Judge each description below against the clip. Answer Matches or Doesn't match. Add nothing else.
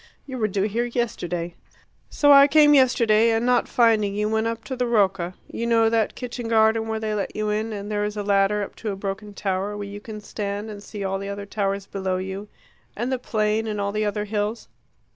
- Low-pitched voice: Doesn't match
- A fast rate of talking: Matches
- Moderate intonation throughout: Doesn't match